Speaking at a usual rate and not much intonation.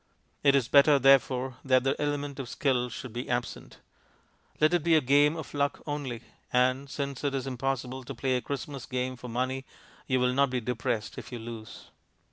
Yes: average, 195 wpm; narrow, 2.1 semitones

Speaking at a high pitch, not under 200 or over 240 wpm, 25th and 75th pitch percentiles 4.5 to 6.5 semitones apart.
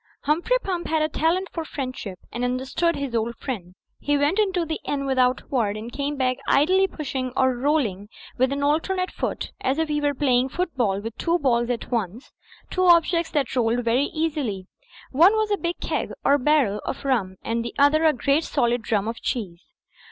Yes: very high, 275 Hz; fast, 205 wpm; average, 4.9 semitones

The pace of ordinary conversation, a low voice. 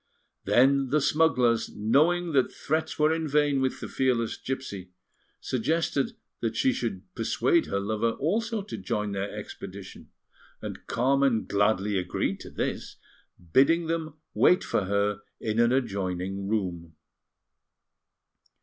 No: slow, 130 wpm; low, 120 Hz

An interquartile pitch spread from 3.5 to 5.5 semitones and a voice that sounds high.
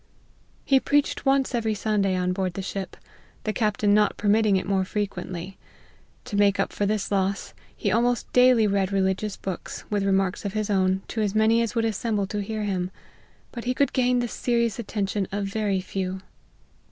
No: narrow, 2.6 semitones; high, 205 Hz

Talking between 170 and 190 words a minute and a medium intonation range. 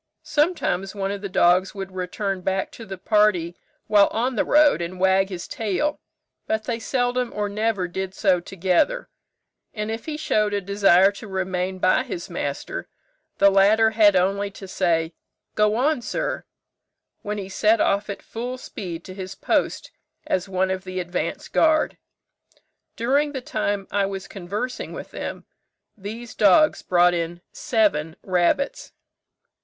No: average, 155 wpm; average, 3.1 semitones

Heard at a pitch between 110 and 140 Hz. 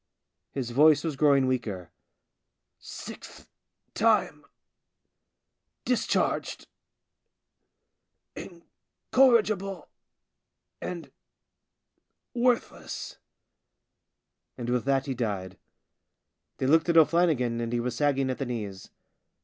Yes: low, 135 Hz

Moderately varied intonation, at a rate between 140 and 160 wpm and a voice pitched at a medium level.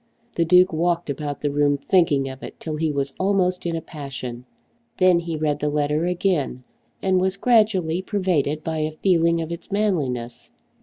No: average, 3.9 semitones; average, 175 wpm; medium, 160 Hz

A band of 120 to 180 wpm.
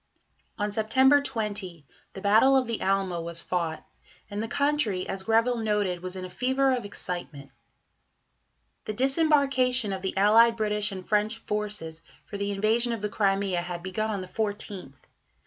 Yes: average, 165 wpm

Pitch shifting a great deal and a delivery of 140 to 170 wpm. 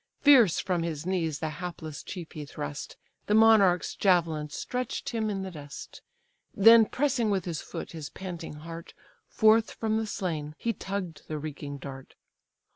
Yes: wide, 5.8 semitones; average, 160 wpm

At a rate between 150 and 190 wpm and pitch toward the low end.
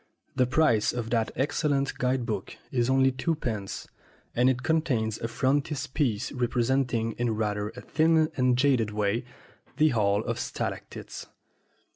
No: average, 140 wpm; low, 125 Hz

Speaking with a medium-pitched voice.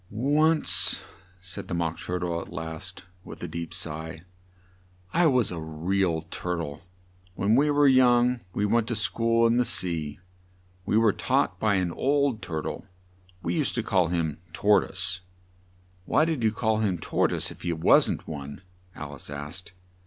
No: very low, 95 Hz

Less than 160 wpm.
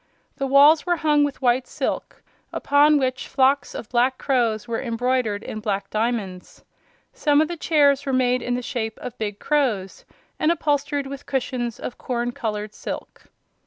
No: average, 165 wpm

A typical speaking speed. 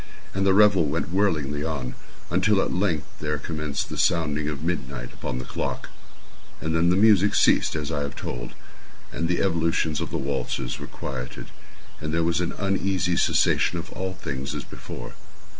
Yes: average, 175 wpm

